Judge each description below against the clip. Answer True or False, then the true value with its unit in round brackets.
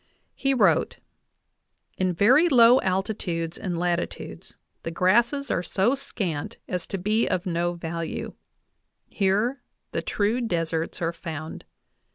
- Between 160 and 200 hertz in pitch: True (185 Hz)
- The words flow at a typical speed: False (125 wpm)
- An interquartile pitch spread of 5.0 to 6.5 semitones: True (5.4 semitones)